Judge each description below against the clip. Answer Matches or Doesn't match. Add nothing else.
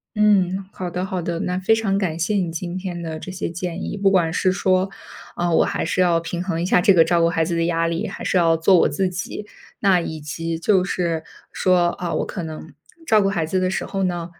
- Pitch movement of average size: Doesn't match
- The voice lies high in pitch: Doesn't match